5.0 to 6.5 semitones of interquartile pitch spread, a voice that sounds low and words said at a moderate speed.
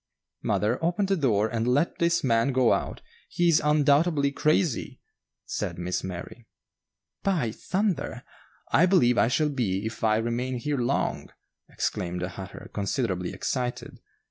Yes: wide, 5.6 semitones; low, 125 Hz; average, 145 wpm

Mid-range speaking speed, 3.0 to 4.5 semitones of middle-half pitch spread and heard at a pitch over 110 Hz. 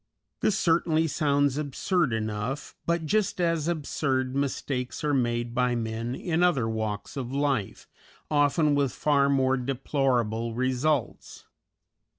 No: slow, 125 wpm; average, 3.9 semitones; low, 135 Hz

